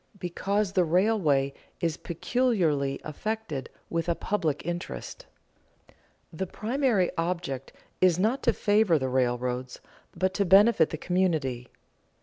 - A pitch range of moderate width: No, wide, 5.8 semitones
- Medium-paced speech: No, slow, 120 wpm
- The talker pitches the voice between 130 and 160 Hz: No, medium, 175 Hz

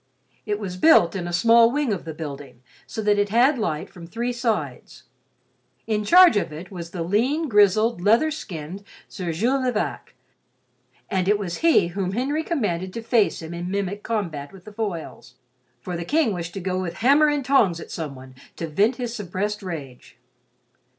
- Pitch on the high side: Yes, high, 200 Hz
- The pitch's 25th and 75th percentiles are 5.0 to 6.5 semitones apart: Yes, average, 5.3 semitones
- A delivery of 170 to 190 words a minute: Yes, average, 185 wpm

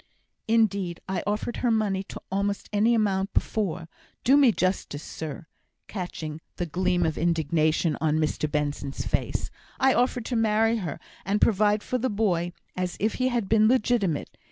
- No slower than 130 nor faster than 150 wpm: No, average, 160 wpm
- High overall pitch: Yes, high, 195 Hz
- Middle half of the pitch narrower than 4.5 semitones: No, average, 5.0 semitones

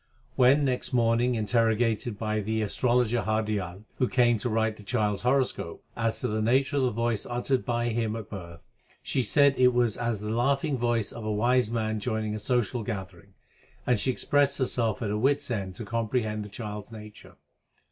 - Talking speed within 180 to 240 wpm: Yes, average, 195 wpm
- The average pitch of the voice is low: Yes, low, 115 Hz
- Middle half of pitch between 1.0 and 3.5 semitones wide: Yes, average, 2.7 semitones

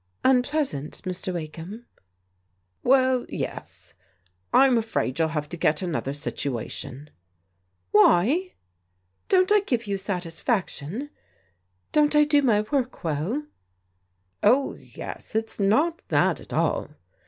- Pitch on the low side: No, high, 200 Hz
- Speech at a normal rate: No, slow, 130 wpm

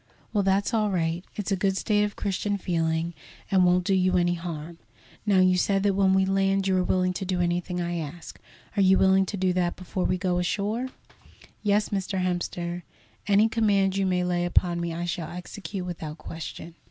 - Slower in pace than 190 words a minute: No, average, 200 wpm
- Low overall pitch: No, medium, 185 Hz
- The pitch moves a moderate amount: No, narrow, 2.0 semitones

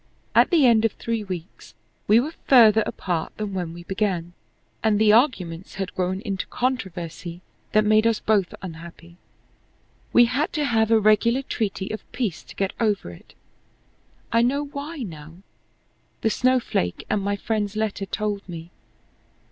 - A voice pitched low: No, high, 210 Hz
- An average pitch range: Yes, average, 4.0 semitones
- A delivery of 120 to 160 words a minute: Yes, average, 155 wpm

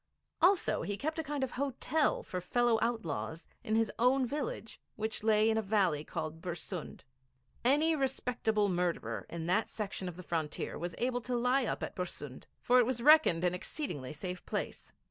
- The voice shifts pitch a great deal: Yes, wide, 6.2 semitones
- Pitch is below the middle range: No, high, 220 Hz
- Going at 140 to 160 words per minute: No, average, 180 wpm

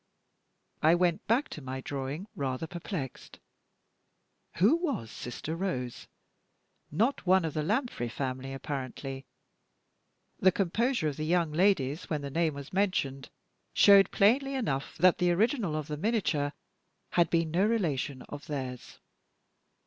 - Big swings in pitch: Yes, wide, 6.1 semitones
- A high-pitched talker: No, medium, 160 Hz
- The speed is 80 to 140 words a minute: Yes, slow, 135 wpm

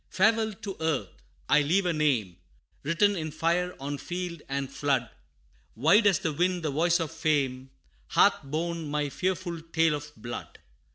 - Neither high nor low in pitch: Yes, medium, 160 Hz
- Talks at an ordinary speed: Yes, average, 160 wpm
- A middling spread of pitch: Yes, average, 3.7 semitones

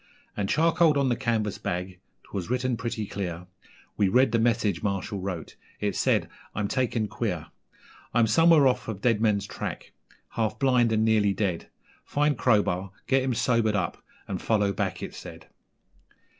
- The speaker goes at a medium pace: Yes, average, 155 wpm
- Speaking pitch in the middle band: No, low, 110 Hz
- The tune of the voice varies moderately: Yes, average, 3.6 semitones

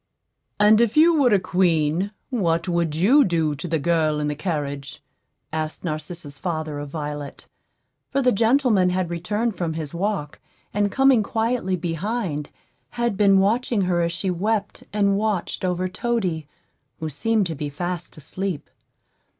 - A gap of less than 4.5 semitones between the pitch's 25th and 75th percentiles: No, average, 4.9 semitones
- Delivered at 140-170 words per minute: Yes, average, 155 wpm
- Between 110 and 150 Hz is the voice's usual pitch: No, medium, 180 Hz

